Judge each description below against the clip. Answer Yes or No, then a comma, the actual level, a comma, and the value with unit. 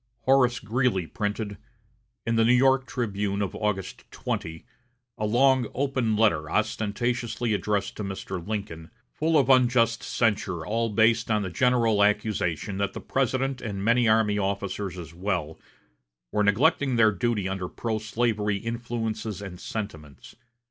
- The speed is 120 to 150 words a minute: Yes, average, 140 wpm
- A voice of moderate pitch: No, low, 110 Hz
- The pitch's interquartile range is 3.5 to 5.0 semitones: No, average, 3.1 semitones